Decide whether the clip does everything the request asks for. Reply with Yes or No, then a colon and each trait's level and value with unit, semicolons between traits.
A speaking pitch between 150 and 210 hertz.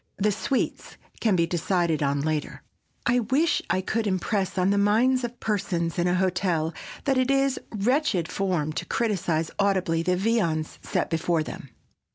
Yes: high, 190 Hz